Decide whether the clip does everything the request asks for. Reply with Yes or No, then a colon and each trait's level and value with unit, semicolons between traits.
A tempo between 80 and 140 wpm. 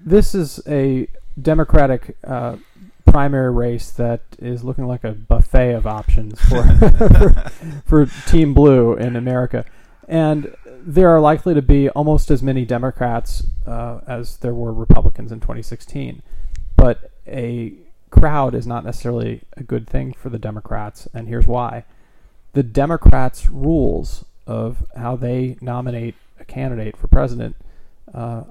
Yes: slow, 135 wpm